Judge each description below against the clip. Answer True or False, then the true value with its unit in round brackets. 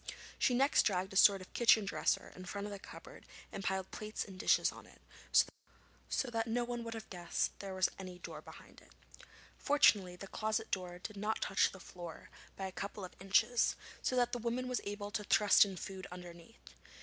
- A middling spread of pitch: True (3.4 semitones)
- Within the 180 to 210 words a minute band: True (200 wpm)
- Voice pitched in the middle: False (200 Hz)